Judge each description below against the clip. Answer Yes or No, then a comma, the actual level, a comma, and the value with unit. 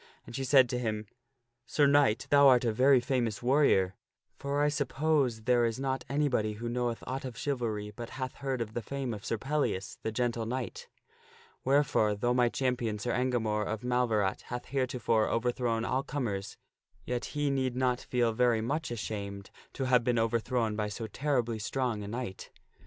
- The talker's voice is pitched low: Yes, low, 125 Hz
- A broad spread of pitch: No, average, 3.0 semitones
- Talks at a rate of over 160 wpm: Yes, average, 180 wpm